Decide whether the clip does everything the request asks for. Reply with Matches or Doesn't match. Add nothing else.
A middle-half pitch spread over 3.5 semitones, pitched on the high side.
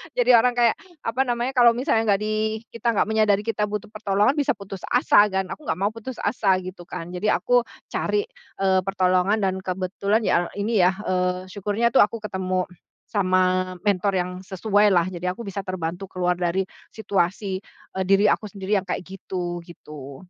Doesn't match